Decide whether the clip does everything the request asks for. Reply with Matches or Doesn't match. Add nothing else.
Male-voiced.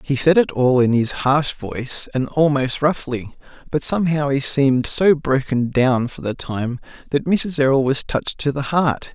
Matches